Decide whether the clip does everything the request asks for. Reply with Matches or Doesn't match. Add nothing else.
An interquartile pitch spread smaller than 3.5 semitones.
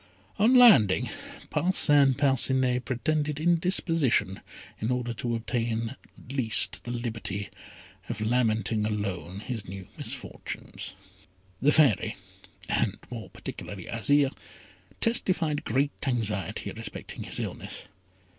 Doesn't match